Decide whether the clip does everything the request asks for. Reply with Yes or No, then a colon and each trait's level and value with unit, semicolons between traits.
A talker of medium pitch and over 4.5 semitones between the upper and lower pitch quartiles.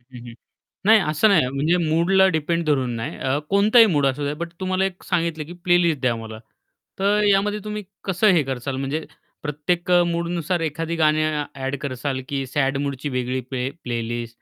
Yes: medium, 155 Hz; average, 4.9 semitones